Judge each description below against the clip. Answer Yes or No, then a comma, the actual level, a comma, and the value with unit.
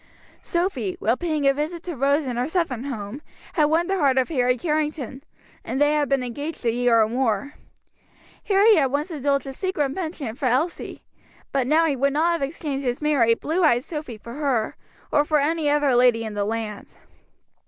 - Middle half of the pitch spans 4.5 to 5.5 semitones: No, average, 4.0 semitones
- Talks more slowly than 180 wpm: No, average, 200 wpm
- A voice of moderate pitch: No, very high, 280 Hz